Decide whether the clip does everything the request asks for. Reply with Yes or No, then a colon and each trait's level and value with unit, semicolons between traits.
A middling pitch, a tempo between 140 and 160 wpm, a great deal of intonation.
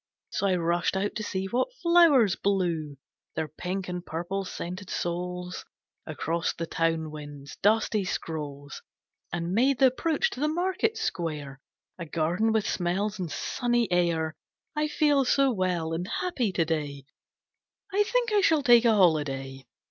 Yes: medium, 180 Hz; average, 155 wpm; wide, 6.8 semitones